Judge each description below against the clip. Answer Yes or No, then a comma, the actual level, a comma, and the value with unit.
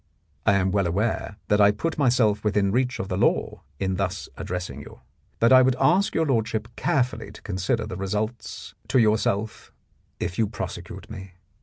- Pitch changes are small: No, average, 3.7 semitones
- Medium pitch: No, low, 105 Hz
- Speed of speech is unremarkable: Yes, average, 175 wpm